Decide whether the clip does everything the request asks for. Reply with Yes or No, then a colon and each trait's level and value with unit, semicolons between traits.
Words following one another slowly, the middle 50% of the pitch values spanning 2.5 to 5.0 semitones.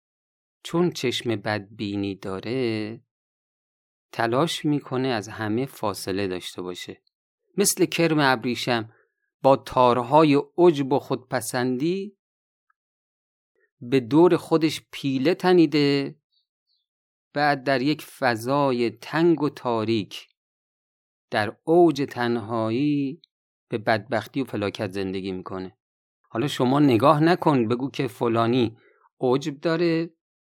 No: slow, 95 wpm; wide, 5.4 semitones